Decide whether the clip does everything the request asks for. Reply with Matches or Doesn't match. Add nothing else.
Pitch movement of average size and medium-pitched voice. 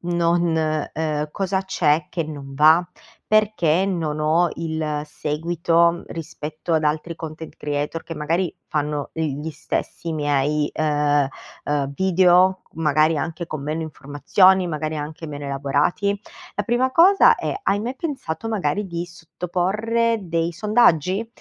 Matches